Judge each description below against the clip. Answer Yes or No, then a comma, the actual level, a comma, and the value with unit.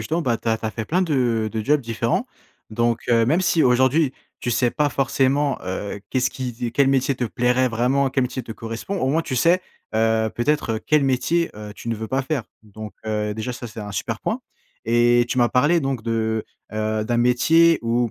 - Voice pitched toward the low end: Yes, low, 120 Hz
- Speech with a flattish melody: No, average, 3.5 semitones